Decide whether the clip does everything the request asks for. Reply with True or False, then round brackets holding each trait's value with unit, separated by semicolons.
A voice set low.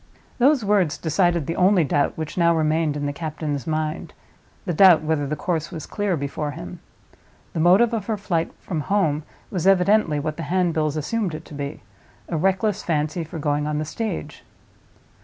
False (160 Hz)